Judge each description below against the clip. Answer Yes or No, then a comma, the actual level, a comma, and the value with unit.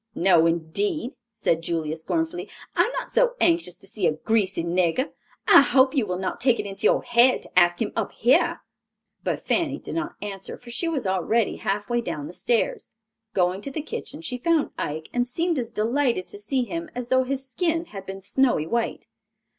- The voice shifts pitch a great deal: Yes, wide, 6.7 semitones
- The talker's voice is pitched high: Yes, high, 235 Hz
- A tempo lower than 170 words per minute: No, average, 200 wpm